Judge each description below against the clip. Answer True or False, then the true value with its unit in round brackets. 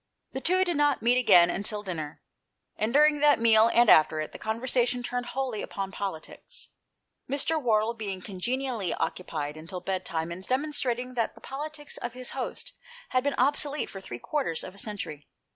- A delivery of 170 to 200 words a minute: True (175 wpm)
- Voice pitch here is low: False (230 Hz)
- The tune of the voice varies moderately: False (6.0 semitones)